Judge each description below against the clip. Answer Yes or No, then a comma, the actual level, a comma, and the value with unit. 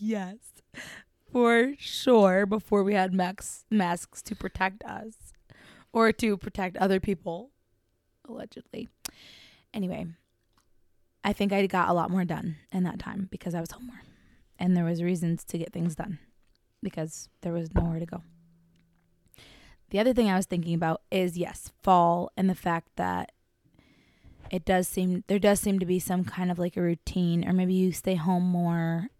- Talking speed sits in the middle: Yes, average, 170 wpm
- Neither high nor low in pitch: Yes, medium, 180 Hz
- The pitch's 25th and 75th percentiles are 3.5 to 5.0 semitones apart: No, average, 2.7 semitones